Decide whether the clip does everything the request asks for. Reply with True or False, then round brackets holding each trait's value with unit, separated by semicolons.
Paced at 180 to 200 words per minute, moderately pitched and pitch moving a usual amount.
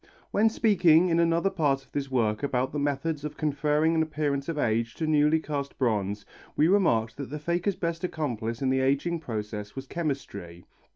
True (185 wpm; 145 Hz; 4.6 semitones)